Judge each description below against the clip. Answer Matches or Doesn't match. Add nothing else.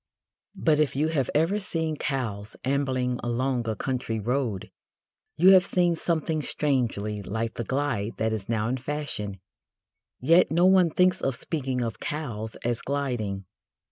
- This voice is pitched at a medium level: Doesn't match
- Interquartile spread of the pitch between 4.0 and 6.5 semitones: Matches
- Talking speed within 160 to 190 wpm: Doesn't match